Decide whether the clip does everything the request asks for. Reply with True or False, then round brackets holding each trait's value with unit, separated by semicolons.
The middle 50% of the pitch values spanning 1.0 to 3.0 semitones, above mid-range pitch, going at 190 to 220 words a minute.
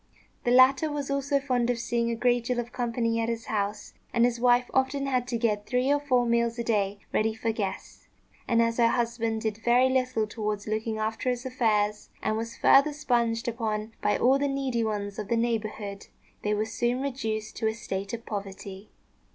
True (2.5 semitones; 230 Hz; 200 wpm)